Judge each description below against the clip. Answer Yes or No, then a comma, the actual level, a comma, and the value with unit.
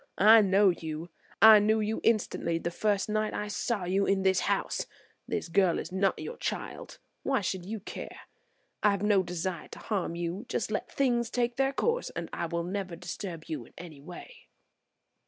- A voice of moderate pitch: No, high, 195 Hz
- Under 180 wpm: No, average, 190 wpm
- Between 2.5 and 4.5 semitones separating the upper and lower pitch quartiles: Yes, average, 3.7 semitones